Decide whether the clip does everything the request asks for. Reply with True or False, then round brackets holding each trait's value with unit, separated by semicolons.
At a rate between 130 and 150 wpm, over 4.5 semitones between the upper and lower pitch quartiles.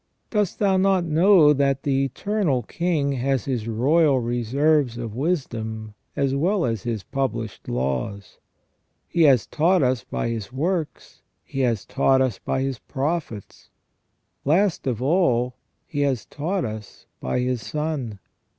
True (140 wpm; 5.2 semitones)